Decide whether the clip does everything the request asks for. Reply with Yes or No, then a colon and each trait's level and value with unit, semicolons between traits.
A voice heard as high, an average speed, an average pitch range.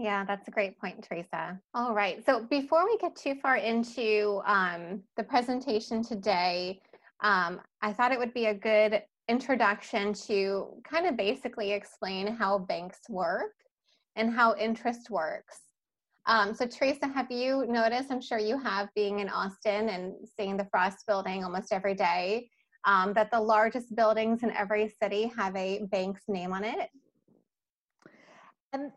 Yes: high, 215 Hz; average, 155 wpm; average, 3.3 semitones